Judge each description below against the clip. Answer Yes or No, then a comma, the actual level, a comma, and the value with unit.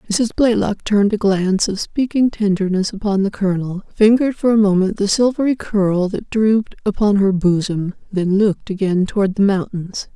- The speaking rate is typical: Yes, average, 170 wpm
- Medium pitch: No, high, 205 Hz